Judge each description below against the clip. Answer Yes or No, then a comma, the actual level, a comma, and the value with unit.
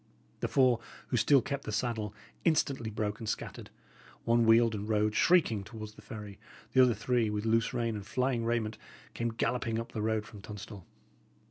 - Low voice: Yes, low, 115 Hz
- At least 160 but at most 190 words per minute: Yes, average, 180 wpm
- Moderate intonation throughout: No, narrow, 2.1 semitones